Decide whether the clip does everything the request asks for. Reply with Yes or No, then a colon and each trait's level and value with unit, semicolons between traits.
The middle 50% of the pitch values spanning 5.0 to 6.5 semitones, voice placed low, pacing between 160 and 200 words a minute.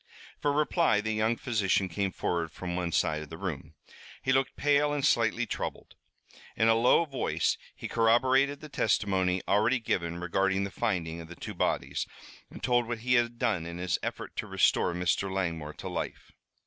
Yes: wide, 5.5 semitones; low, 105 Hz; average, 185 wpm